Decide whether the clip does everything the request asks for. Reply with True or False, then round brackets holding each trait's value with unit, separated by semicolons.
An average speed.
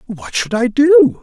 True (195 wpm)